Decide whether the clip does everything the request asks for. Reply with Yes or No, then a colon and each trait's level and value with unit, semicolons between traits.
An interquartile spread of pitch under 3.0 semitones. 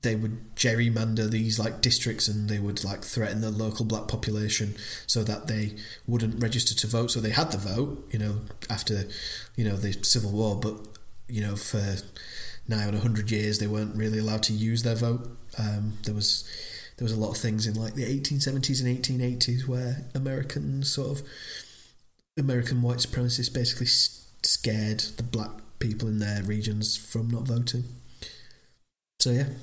Yes: narrow, 2.4 semitones